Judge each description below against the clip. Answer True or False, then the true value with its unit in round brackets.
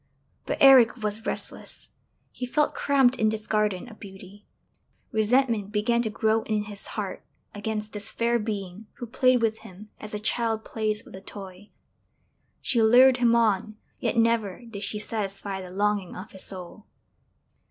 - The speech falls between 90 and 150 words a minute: False (165 wpm)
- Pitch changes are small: True (2.3 semitones)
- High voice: True (215 Hz)